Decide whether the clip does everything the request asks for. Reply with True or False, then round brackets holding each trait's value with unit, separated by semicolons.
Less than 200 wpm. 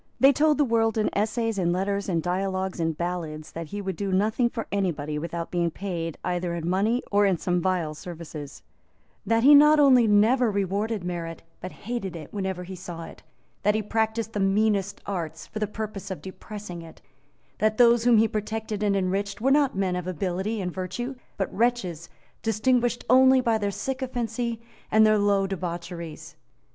True (180 wpm)